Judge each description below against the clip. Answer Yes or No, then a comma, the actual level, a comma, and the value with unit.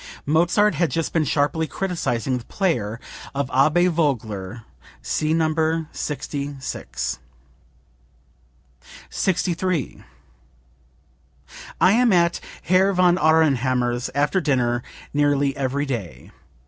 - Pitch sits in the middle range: Yes, medium, 145 Hz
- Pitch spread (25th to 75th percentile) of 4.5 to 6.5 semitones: Yes, average, 5.3 semitones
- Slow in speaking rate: Yes, slow, 95 wpm